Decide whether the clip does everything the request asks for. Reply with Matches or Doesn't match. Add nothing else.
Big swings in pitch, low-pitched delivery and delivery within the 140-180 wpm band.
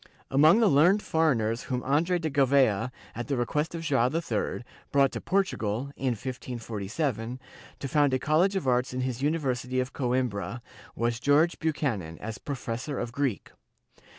Doesn't match